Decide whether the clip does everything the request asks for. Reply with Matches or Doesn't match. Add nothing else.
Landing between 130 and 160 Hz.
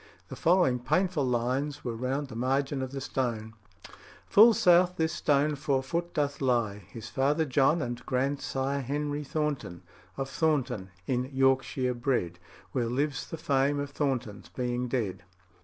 Matches